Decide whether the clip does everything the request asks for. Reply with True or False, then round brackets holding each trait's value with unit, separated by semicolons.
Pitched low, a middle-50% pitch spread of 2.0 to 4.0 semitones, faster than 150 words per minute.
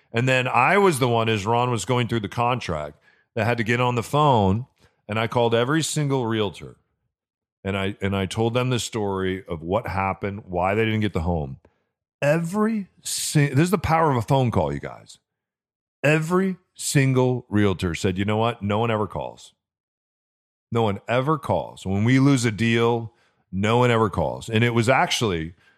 False (115 Hz; 4.8 semitones; 190 wpm)